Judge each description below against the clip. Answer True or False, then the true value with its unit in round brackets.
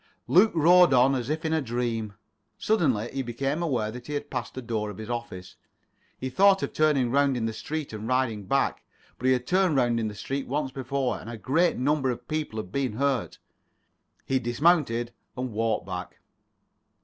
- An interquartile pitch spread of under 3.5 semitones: False (4.0 semitones)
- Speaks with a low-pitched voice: True (130 Hz)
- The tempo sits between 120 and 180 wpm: False (195 wpm)